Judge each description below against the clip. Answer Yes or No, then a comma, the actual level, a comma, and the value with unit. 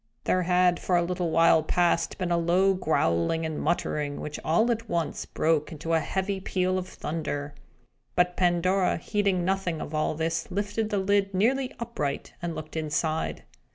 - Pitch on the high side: No, medium, 175 Hz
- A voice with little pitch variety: No, average, 3.2 semitones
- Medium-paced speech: Yes, average, 170 wpm